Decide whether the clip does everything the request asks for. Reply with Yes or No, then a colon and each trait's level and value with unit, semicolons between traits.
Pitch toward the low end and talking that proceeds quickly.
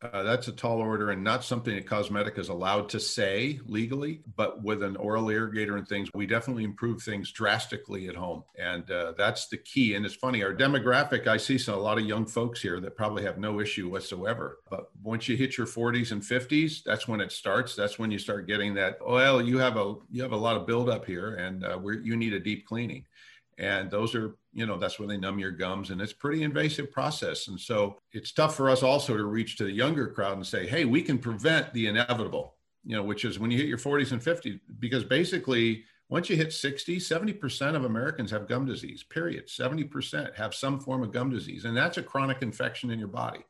Yes: low, 115 Hz; fast, 230 wpm